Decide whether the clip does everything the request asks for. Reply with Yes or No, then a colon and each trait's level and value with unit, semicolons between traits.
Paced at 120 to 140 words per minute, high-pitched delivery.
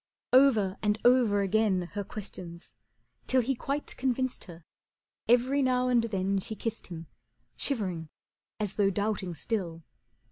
Yes: slow, 135 wpm; high, 210 Hz